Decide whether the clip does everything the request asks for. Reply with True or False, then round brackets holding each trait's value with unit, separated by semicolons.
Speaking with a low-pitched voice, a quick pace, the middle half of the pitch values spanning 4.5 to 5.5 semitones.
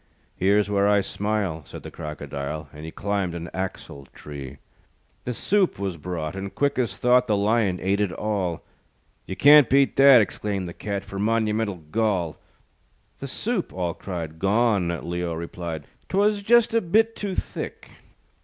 False (100 Hz; 160 wpm; 5.0 semitones)